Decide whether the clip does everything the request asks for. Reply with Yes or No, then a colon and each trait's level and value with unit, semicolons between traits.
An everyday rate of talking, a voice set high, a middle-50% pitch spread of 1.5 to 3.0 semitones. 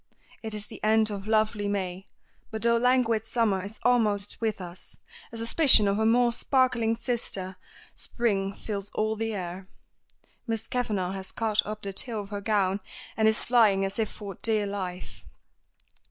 Yes: average, 170 wpm; high, 215 Hz; narrow, 2.4 semitones